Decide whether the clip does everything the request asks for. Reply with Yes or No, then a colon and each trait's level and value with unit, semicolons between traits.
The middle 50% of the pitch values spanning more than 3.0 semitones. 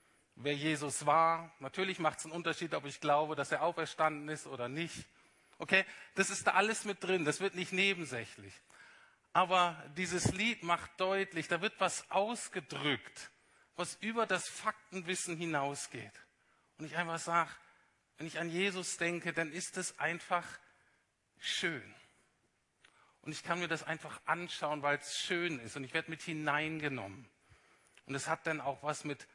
Yes: average, 3.7 semitones